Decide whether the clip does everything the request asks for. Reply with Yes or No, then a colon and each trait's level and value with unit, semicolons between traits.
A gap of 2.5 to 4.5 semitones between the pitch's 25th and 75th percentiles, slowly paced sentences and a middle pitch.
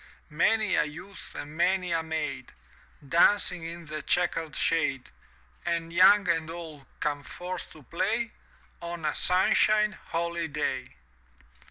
Yes: average, 2.8 semitones; slow, 130 wpm; medium, 170 Hz